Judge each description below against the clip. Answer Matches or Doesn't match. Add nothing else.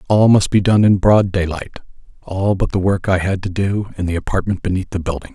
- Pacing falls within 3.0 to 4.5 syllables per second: Doesn't match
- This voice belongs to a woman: Doesn't match